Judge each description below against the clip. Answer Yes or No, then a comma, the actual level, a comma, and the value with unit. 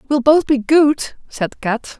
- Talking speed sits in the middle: Yes, average, 180 wpm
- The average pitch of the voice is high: Yes, very high, 265 Hz